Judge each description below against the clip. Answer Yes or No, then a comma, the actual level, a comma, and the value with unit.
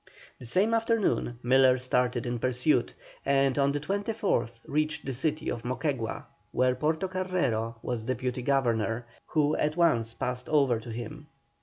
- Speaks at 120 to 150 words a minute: Yes, average, 145 wpm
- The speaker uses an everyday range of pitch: Yes, average, 4.1 semitones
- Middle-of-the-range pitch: No, low, 130 Hz